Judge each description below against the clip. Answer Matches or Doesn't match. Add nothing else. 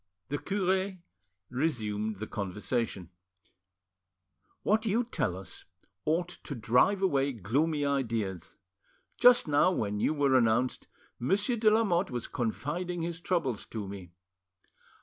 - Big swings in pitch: Matches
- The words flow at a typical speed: Doesn't match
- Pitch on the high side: Doesn't match